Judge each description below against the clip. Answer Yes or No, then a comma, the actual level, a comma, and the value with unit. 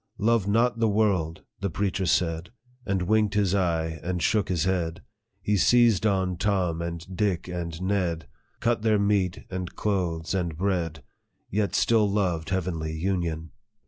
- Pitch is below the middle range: Yes, very low, 95 Hz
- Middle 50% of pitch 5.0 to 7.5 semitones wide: No, average, 3.4 semitones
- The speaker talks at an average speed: Yes, average, 160 wpm